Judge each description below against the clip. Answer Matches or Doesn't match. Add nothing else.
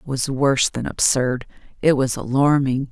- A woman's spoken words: Matches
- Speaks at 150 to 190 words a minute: Matches